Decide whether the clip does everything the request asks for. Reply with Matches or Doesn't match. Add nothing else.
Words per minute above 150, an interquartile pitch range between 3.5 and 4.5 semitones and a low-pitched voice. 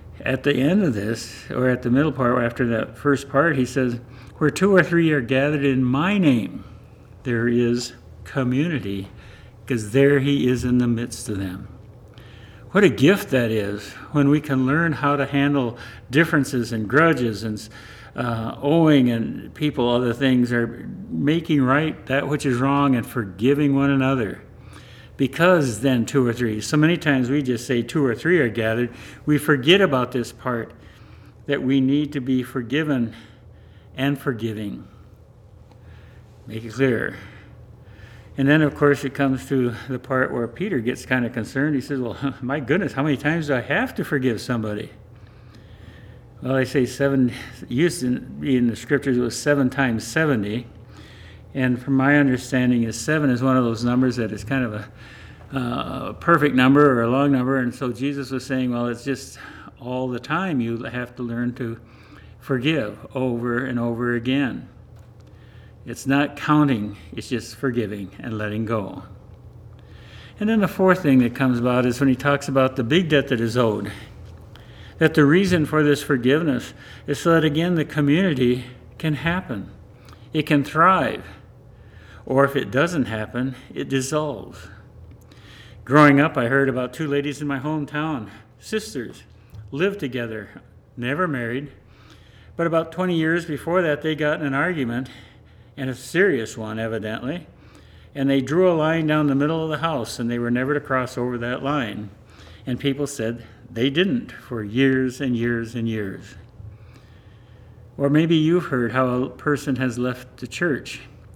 Matches